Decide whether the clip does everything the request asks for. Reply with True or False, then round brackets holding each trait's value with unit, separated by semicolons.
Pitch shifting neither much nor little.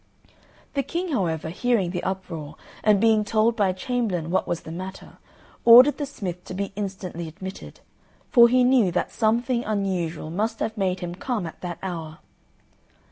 True (4.7 semitones)